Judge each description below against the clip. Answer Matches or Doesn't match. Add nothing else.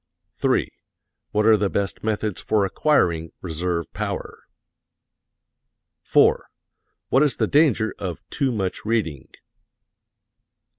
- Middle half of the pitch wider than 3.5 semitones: Matches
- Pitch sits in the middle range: Doesn't match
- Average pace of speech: Doesn't match